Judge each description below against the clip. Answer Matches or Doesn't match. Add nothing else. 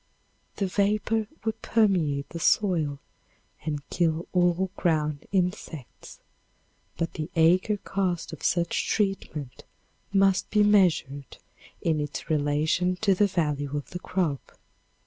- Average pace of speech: Doesn't match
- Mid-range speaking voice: Matches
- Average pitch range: Matches